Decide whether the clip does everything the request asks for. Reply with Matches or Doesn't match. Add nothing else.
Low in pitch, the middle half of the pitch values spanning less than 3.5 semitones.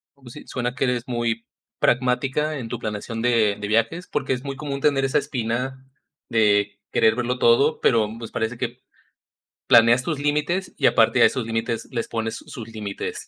Matches